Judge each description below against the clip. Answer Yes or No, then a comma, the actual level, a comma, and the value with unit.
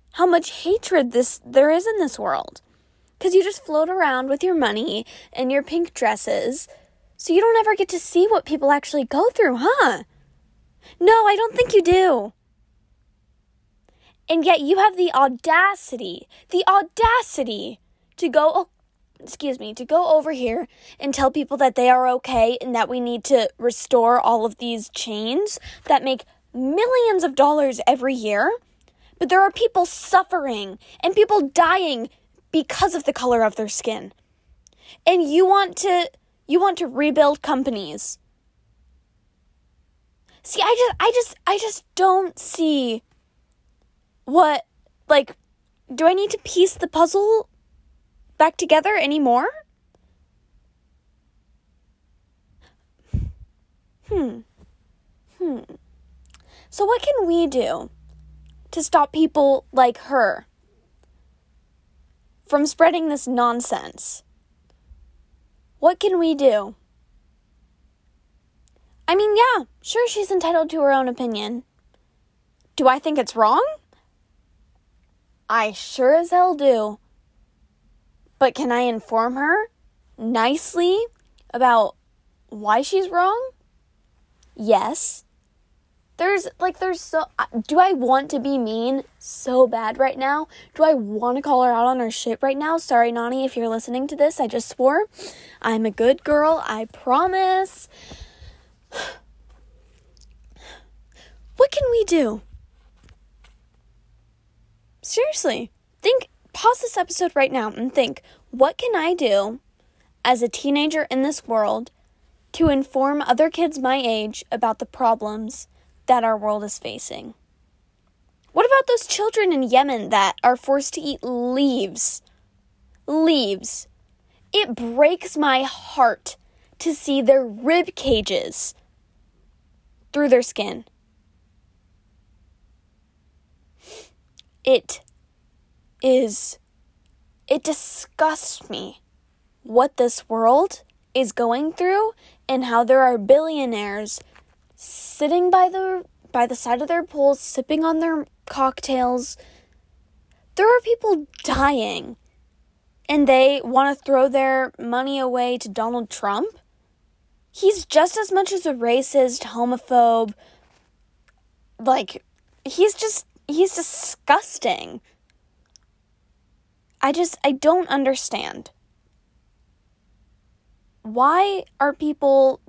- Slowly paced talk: Yes, slow, 120 wpm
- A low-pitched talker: No, very high, 270 Hz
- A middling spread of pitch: No, wide, 7.1 semitones